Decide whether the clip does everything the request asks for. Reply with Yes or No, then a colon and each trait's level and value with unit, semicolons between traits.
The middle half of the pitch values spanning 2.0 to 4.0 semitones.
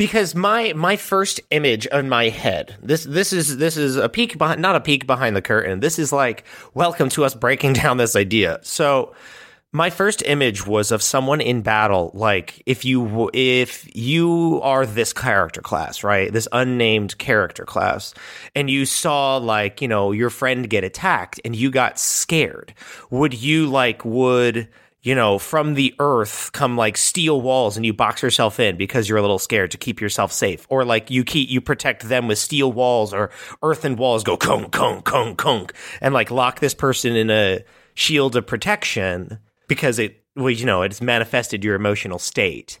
No: average, 4.4 semitones